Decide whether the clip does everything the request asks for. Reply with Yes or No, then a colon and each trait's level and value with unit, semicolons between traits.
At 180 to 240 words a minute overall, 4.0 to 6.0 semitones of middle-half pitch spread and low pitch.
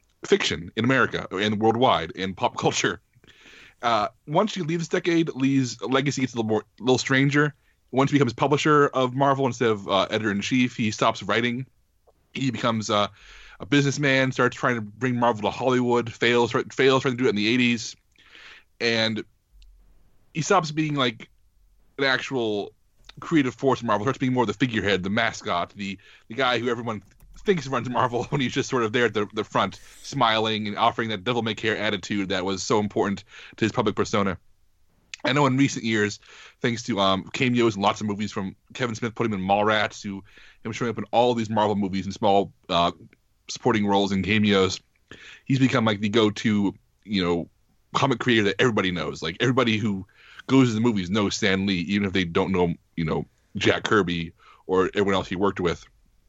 Yes: average, 195 wpm; average, 4.4 semitones; low, 115 Hz